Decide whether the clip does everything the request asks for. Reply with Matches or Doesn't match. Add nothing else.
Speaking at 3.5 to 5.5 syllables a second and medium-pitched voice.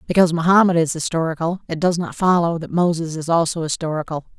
Doesn't match